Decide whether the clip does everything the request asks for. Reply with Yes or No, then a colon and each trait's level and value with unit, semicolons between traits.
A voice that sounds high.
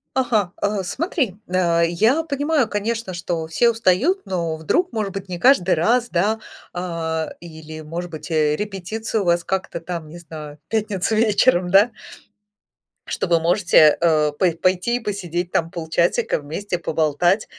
No: medium, 180 Hz